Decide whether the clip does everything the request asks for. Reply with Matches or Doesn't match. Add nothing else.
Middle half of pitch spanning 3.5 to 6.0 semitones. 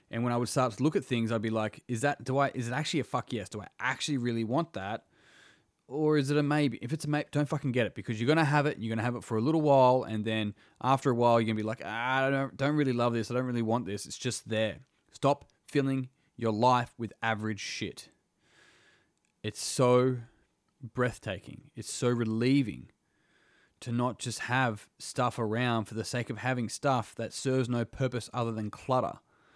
Doesn't match